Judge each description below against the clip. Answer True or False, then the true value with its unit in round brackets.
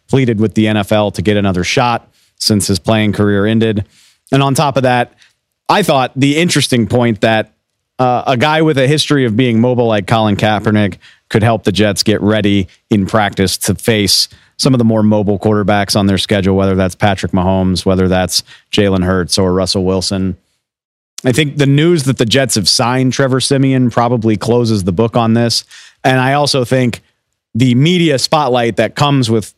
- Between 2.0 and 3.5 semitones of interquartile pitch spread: False (4.0 semitones)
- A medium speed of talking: True (190 wpm)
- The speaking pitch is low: True (110 Hz)